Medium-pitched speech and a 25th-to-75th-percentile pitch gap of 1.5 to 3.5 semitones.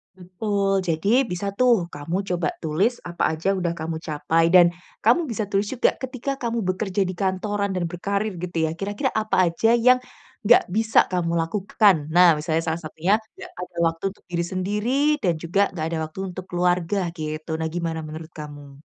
No: medium, 180 Hz; average, 3.9 semitones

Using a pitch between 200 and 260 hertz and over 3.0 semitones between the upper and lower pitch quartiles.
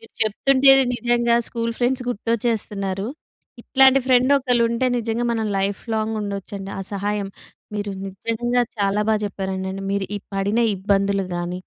Yes: high, 215 Hz; average, 3.4 semitones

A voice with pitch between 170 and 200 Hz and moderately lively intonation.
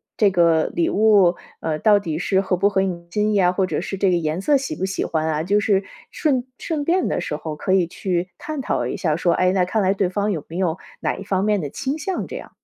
Yes: high, 190 Hz; average, 3.2 semitones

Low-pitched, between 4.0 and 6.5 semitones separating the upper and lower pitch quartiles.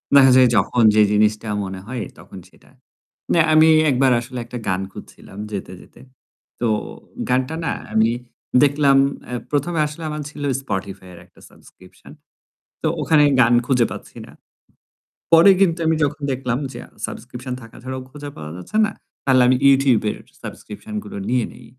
Yes: low, 125 Hz; average, 4.7 semitones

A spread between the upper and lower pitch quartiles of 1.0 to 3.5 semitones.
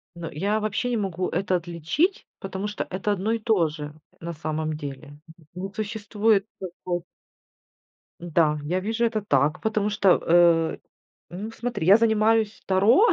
No: average, 4.4 semitones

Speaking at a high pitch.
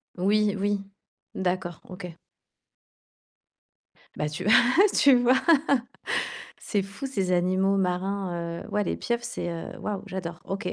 Yes: high, 195 Hz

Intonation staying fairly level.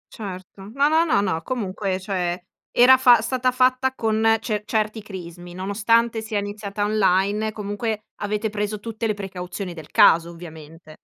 No: average, 3.2 semitones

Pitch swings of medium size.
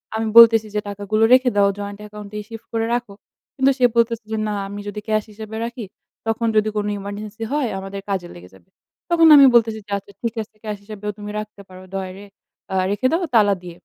No: narrow, 2.1 semitones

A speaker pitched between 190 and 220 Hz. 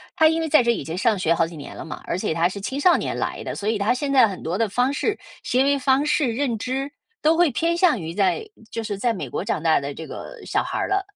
No: high, 235 Hz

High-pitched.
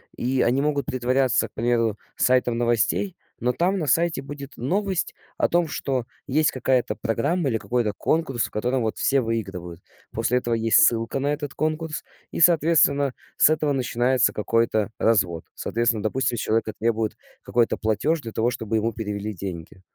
No: low, 120 Hz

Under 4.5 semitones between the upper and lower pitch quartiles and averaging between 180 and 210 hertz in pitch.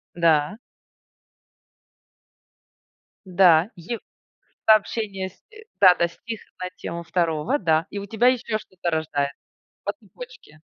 No: average, 4.9 semitones; medium, 185 Hz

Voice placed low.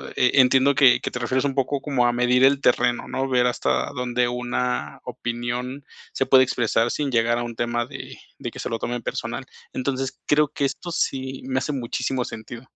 Yes: low, 125 Hz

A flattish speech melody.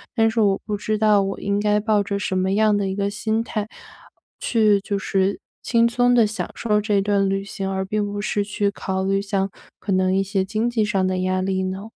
Yes: narrow, 1.8 semitones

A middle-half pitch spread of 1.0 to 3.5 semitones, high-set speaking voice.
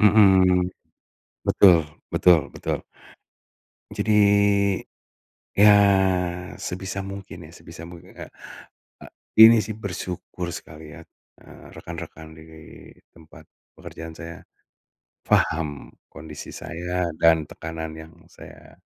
No: average, 3.1 semitones; very low, 85 Hz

